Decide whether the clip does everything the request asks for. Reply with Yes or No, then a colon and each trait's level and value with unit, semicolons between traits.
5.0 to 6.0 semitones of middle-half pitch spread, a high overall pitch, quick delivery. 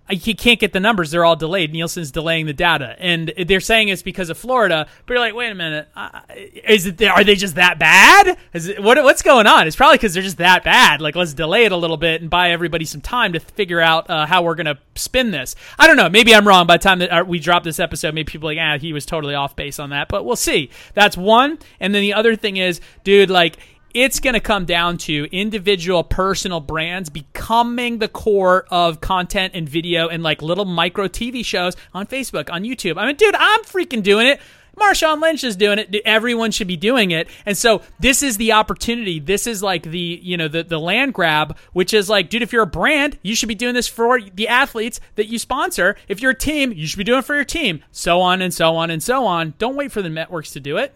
Yes: wide, 5.5 semitones; high, 195 Hz; fast, 250 wpm